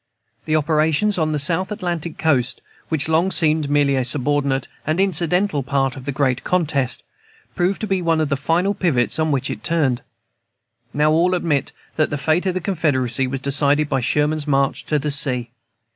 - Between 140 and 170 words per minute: No, average, 185 wpm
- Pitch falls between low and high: Yes, medium, 150 Hz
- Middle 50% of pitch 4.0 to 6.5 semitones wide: No, average, 3.4 semitones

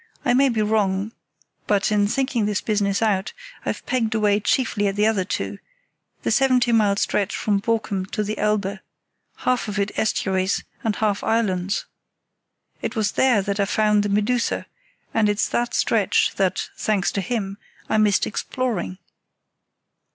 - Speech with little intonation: Yes, narrow, 2.0 semitones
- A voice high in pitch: Yes, high, 210 Hz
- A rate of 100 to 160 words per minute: Yes, average, 155 wpm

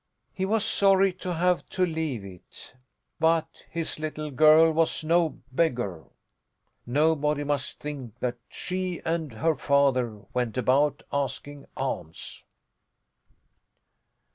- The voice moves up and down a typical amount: Yes, average, 4.3 semitones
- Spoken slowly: Yes, slow, 115 wpm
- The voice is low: No, medium, 150 Hz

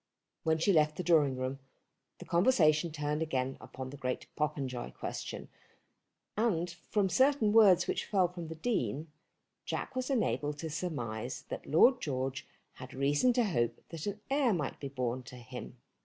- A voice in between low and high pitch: Yes, medium, 155 Hz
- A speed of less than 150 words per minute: No, average, 165 wpm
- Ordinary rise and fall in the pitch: No, wide, 6.2 semitones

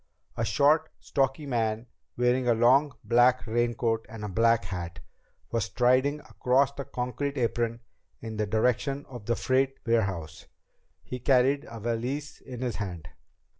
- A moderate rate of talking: Yes, average, 145 wpm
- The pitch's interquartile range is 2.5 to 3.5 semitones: Yes, average, 2.9 semitones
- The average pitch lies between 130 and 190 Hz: No, low, 120 Hz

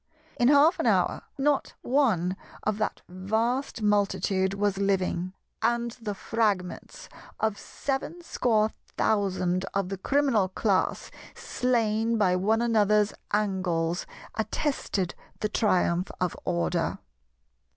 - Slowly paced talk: Yes, slow, 110 wpm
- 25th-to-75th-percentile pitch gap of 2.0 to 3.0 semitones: No, average, 3.7 semitones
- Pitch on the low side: No, high, 210 Hz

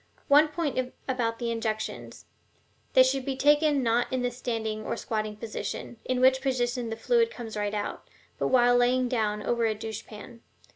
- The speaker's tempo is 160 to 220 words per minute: Yes, average, 180 wpm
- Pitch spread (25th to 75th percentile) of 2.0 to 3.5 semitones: Yes, average, 2.8 semitones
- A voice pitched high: Yes, high, 245 Hz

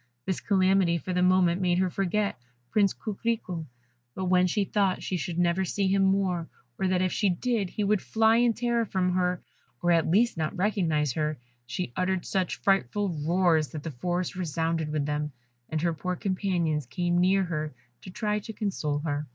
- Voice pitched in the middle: Yes, medium, 180 Hz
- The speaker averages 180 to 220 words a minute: Yes, average, 190 wpm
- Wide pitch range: No, average, 3.0 semitones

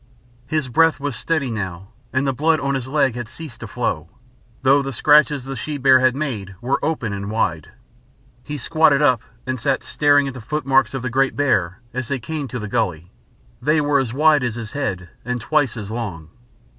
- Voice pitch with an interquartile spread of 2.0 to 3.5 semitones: No, average, 4.2 semitones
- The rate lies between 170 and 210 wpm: Yes, fast, 205 wpm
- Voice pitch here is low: Yes, low, 130 Hz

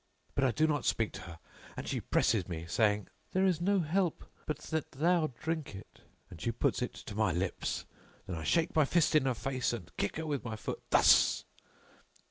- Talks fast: Yes, fast, 210 wpm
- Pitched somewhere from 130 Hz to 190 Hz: Yes, low, 135 Hz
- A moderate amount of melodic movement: No, wide, 7.6 semitones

